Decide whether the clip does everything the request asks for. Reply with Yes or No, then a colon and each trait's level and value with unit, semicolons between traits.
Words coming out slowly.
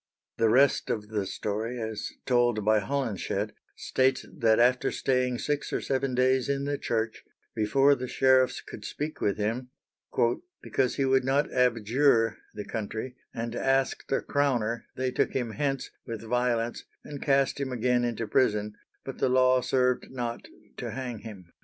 No: average, 160 wpm